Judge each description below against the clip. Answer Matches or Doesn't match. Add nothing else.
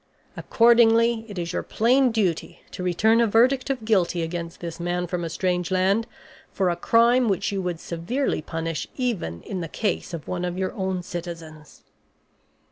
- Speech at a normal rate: Matches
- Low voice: Doesn't match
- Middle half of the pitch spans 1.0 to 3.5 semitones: Doesn't match